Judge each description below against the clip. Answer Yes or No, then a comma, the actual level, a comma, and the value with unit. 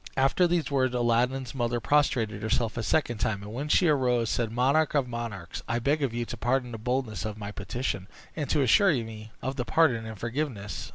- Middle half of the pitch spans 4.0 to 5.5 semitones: No, average, 3.4 semitones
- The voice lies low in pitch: Yes, low, 120 Hz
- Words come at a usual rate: No, fast, 210 wpm